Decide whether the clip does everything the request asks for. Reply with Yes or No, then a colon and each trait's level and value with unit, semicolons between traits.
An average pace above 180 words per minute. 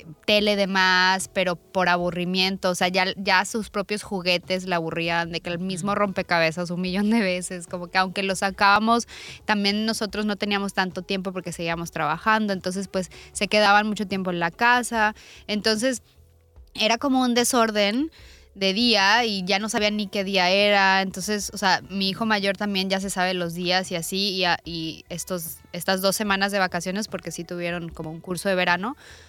Yes: average, 190 wpm